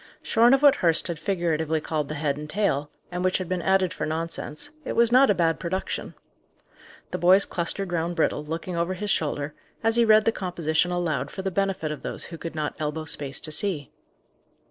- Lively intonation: No, average, 3.7 semitones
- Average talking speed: No, fast, 210 wpm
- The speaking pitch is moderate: Yes, medium, 170 Hz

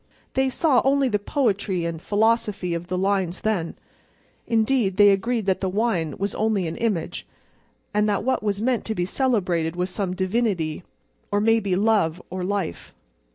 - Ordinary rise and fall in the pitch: Yes, average, 3.7 semitones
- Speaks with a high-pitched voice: Yes, high, 200 Hz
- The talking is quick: No, average, 160 wpm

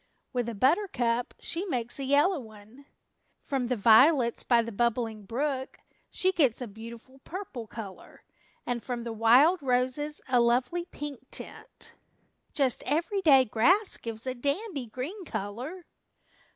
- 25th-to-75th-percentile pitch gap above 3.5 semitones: Yes, average, 4.1 semitones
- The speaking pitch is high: Yes, very high, 255 Hz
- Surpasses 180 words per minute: No, average, 140 wpm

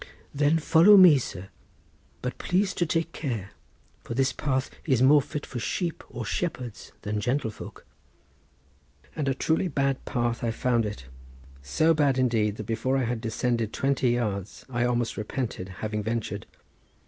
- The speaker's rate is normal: Yes, average, 155 wpm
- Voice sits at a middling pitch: No, low, 125 Hz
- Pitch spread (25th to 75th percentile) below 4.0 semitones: No, average, 4.5 semitones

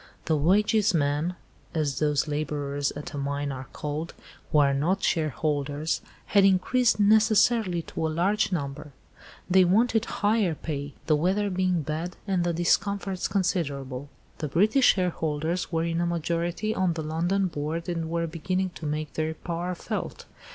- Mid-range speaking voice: Yes, medium, 165 Hz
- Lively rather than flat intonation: No, average, 3.8 semitones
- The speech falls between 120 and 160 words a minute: Yes, average, 150 wpm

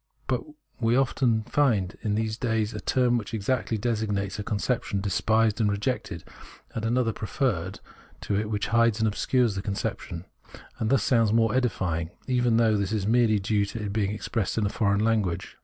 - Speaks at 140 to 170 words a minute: No, average, 190 wpm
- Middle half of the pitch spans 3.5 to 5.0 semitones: No, narrow, 2.4 semitones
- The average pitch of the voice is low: Yes, low, 110 Hz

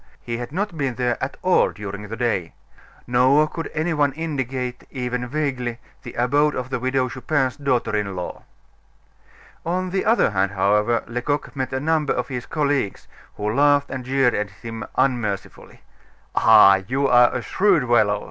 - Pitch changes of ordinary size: Yes, average, 3.6 semitones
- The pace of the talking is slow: No, average, 165 wpm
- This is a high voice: No, low, 125 Hz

